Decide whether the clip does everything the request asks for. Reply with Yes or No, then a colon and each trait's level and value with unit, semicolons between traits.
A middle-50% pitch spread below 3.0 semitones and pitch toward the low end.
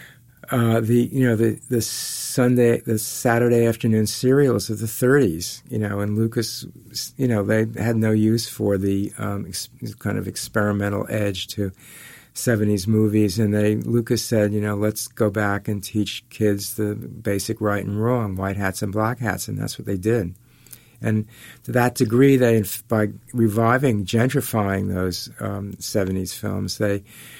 Yes: narrow, 2.5 semitones; low, 110 Hz